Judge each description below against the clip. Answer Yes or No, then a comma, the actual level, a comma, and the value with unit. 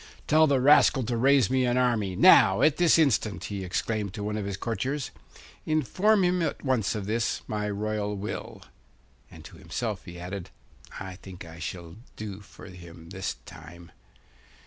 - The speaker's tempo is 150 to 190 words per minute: Yes, average, 170 wpm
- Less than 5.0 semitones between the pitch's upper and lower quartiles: No, wide, 5.5 semitones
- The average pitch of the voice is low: Yes, low, 105 Hz